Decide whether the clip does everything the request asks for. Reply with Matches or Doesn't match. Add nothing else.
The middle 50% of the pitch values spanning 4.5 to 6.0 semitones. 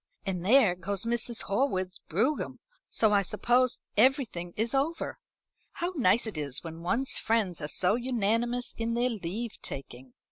Matches